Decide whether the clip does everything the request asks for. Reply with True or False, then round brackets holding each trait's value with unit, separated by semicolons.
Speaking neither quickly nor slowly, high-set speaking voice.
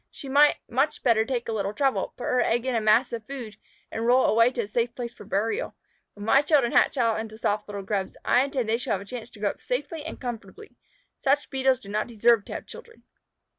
False (245 wpm; 235 Hz)